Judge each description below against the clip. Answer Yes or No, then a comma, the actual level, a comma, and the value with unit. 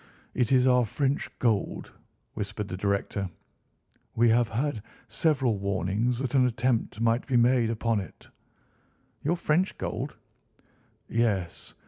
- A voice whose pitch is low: Yes, low, 115 Hz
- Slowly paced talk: Yes, slow, 125 wpm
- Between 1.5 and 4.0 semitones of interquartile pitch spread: Yes, average, 3.5 semitones